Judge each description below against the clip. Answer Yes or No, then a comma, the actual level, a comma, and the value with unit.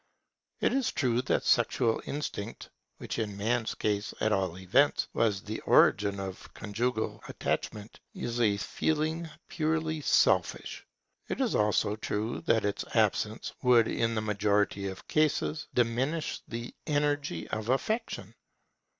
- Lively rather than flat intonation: Yes, wide, 6.0 semitones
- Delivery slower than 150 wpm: Yes, slow, 135 wpm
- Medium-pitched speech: No, low, 115 Hz